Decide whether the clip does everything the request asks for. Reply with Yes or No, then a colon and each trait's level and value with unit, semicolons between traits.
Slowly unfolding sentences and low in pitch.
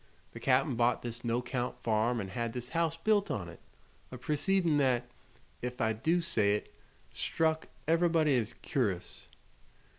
No: average, 150 wpm; low, 125 Hz